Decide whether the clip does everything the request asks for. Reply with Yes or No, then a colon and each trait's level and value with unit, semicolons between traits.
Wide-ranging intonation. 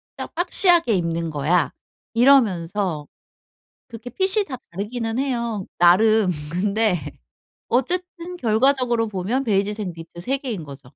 Yes: wide, 6.5 semitones